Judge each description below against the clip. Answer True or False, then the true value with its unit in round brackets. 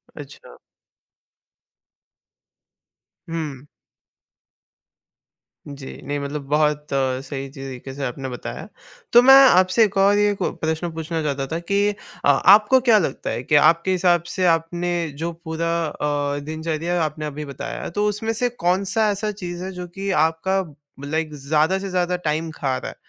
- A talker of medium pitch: True (165 Hz)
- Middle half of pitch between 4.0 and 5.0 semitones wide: True (4.4 semitones)